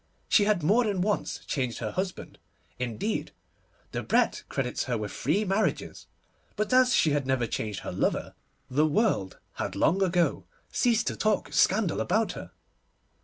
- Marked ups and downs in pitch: Yes, wide, 8.8 semitones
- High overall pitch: No, medium, 175 Hz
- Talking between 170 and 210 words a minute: No, average, 155 wpm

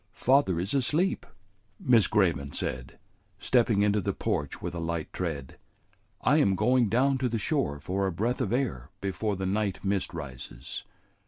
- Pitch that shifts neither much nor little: No, wide, 6.4 semitones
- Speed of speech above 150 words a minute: Yes, average, 165 wpm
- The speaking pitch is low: Yes, low, 100 Hz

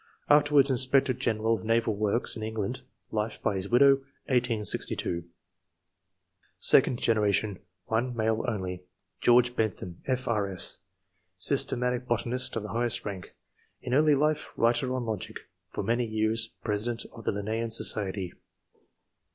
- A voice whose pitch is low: Yes, low, 115 Hz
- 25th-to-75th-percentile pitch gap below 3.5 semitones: Yes, average, 2.8 semitones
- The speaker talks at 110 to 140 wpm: Yes, slow, 135 wpm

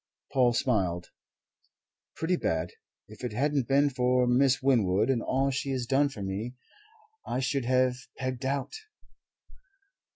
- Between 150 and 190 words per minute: No, slow, 135 wpm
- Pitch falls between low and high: No, low, 130 Hz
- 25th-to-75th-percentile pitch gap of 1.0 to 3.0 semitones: Yes, average, 2.7 semitones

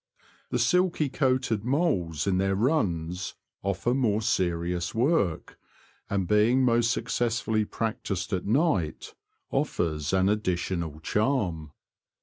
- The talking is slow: Yes, slow, 110 wpm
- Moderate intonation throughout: No, wide, 5.8 semitones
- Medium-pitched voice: No, low, 100 Hz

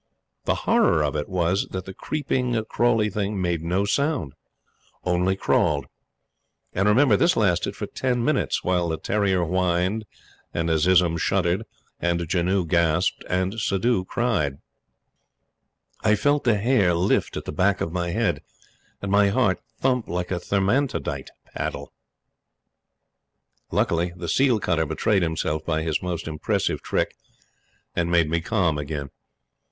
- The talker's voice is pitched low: Yes, very low, 90 Hz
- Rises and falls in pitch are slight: No, average, 3.9 semitones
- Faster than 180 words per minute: No, average, 140 wpm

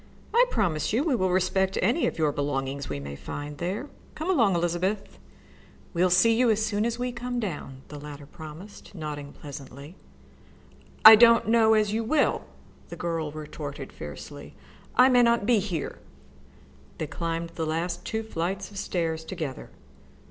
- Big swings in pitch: Yes, wide, 6.6 semitones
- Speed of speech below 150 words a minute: No, average, 155 wpm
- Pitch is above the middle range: No, medium, 180 Hz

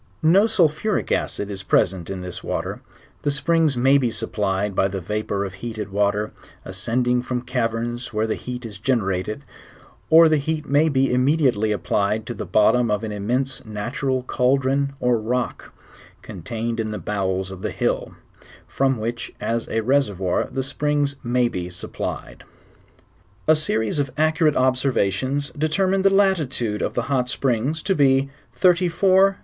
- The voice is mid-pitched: No, low, 125 Hz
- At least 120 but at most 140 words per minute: No, average, 160 wpm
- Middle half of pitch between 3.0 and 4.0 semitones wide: No, average, 5.2 semitones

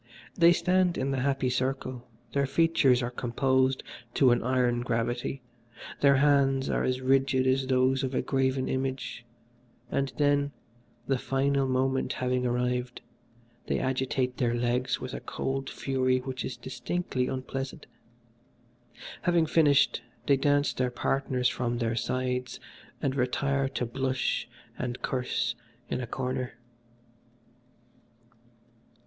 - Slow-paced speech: Yes, slow, 130 wpm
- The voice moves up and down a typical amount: No, narrow, 1.4 semitones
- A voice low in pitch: Yes, low, 130 Hz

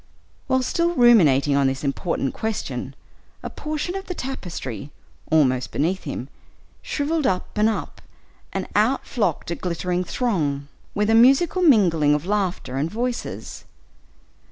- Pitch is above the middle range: Yes, high, 195 Hz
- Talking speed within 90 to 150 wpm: Yes, slow, 135 wpm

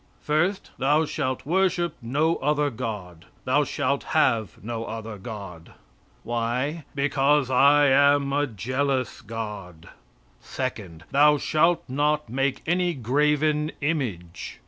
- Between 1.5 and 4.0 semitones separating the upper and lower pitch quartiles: No, average, 4.6 semitones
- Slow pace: Yes, slow, 115 wpm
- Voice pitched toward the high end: No, low, 135 Hz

